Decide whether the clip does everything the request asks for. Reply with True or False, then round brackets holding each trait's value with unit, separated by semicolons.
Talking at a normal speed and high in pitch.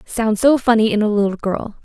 False (260 wpm; 220 Hz)